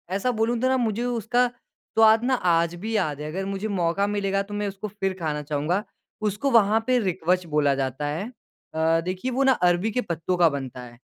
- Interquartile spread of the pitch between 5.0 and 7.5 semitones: Yes, average, 5.3 semitones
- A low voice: No, high, 195 Hz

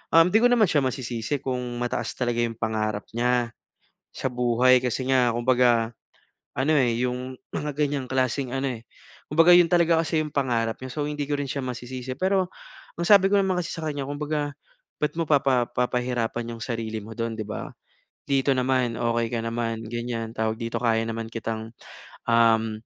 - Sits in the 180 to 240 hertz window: No, low, 125 Hz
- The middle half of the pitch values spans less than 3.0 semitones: No, average, 3.7 semitones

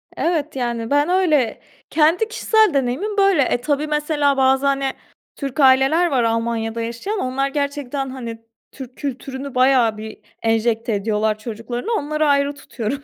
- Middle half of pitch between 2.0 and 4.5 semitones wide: Yes, average, 4.1 semitones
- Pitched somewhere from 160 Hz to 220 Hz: No, very high, 270 Hz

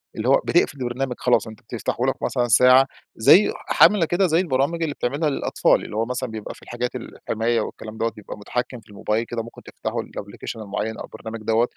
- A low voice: Yes, low, 120 Hz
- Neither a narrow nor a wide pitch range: Yes, average, 3.4 semitones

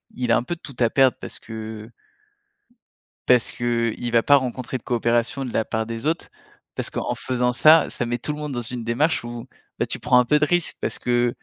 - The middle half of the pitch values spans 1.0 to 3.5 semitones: Yes, narrow, 2.5 semitones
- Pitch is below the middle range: Yes, low, 120 Hz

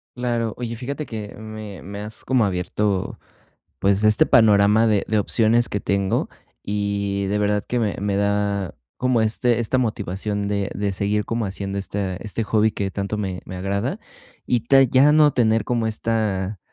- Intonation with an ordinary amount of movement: No, narrow, 2.3 semitones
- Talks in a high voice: No, low, 105 Hz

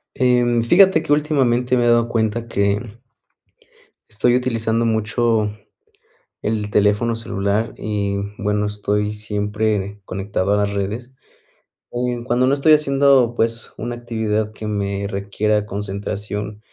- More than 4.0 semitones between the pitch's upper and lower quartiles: No, average, 2.7 semitones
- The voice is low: Yes, low, 110 Hz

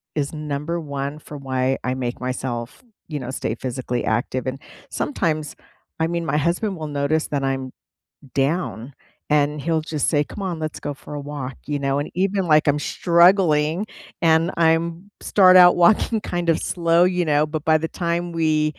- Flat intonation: No, average, 3.3 semitones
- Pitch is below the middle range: No, medium, 155 Hz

